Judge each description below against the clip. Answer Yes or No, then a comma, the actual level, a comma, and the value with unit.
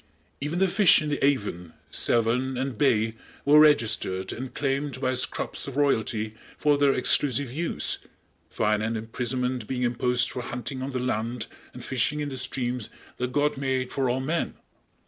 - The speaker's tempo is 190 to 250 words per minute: No, average, 165 wpm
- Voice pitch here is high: No, low, 130 Hz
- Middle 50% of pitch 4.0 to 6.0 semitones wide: No, average, 3.1 semitones